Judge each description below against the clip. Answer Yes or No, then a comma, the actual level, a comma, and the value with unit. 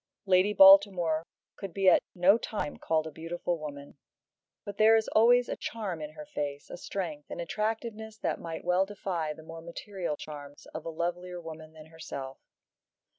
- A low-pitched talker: No, medium, 170 Hz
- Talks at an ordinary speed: Yes, average, 175 wpm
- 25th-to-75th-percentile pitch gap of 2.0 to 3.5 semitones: No, average, 4.0 semitones